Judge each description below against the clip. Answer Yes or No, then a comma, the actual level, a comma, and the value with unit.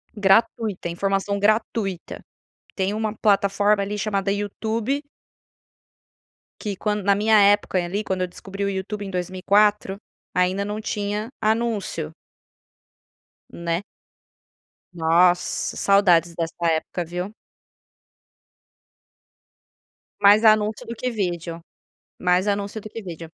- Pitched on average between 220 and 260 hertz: No, high, 200 Hz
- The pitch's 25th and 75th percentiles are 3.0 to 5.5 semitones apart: No, narrow, 2.5 semitones